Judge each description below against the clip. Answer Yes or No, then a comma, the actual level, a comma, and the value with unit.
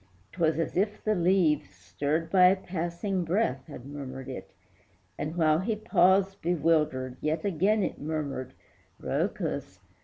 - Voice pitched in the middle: Yes, medium, 165 Hz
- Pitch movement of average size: Yes, average, 4.3 semitones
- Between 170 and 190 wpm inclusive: No, average, 140 wpm